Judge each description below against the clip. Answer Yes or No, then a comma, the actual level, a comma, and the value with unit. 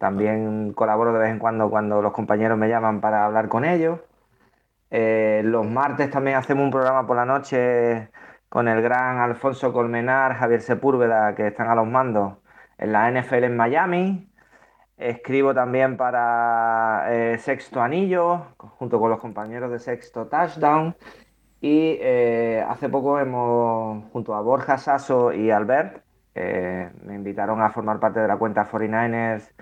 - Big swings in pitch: No, average, 3.1 semitones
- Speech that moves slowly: No, average, 155 wpm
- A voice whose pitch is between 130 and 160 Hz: No, low, 120 Hz